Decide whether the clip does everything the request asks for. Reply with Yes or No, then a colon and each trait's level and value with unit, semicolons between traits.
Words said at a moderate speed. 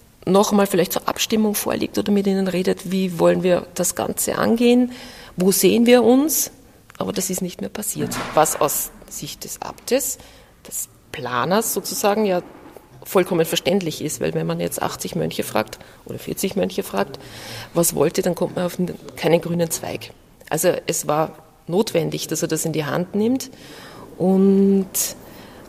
Yes: average, 165 wpm